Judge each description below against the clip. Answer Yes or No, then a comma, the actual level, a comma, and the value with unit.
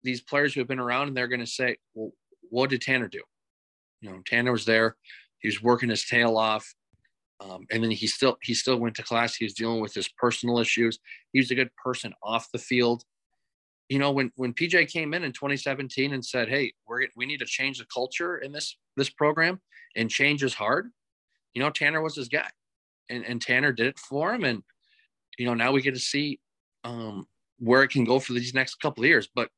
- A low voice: Yes, low, 125 Hz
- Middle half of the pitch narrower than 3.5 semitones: Yes, average, 2.8 semitones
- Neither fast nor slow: No, fast, 225 wpm